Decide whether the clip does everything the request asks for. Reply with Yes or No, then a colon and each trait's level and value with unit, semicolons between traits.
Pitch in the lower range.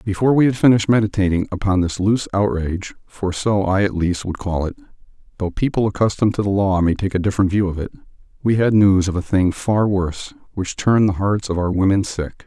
Yes: low, 100 Hz